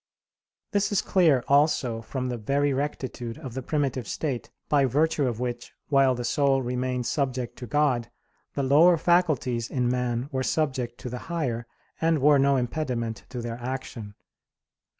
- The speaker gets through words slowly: No, average, 160 wpm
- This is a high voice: No, low, 130 Hz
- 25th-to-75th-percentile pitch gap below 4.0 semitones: Yes, average, 3.1 semitones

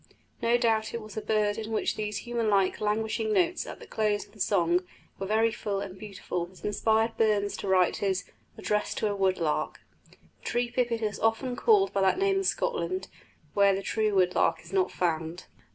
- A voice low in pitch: No, high, 210 Hz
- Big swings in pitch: No, average, 2.7 semitones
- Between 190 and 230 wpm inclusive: Yes, fast, 205 wpm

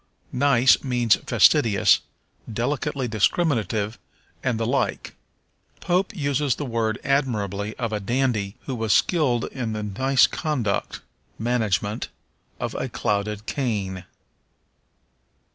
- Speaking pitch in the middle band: No, low, 115 Hz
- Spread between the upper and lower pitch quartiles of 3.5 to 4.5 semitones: Yes, average, 4.2 semitones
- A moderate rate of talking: No, slow, 110 wpm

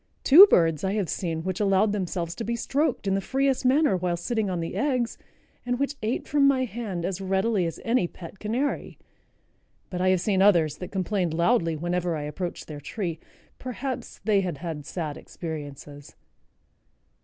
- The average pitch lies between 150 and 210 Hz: Yes, high, 190 Hz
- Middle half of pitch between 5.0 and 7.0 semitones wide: Yes, wide, 5.5 semitones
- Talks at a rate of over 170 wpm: Yes, average, 180 wpm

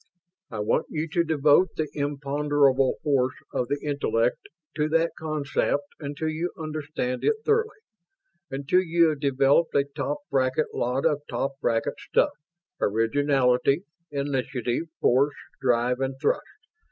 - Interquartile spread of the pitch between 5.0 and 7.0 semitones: No, average, 2.7 semitones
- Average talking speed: No, slow, 130 wpm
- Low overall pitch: No, medium, 145 Hz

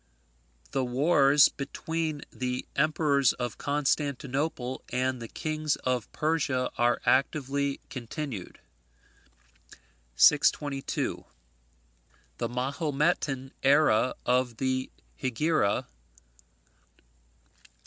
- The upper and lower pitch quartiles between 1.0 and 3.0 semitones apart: Yes, average, 2.7 semitones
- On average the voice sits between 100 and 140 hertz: Yes, low, 135 Hz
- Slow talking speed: Yes, slow, 75 wpm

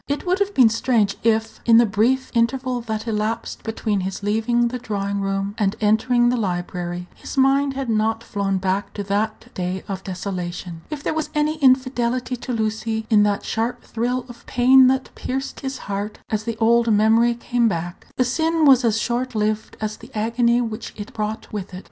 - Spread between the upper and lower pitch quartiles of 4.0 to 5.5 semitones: No, average, 3.3 semitones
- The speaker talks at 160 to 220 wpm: Yes, average, 190 wpm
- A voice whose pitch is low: No, high, 225 Hz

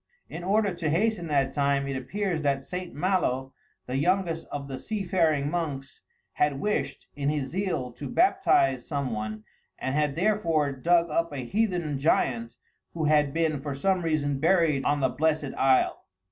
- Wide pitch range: No, average, 4.2 semitones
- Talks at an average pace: Yes, average, 170 wpm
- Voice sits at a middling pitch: Yes, medium, 150 Hz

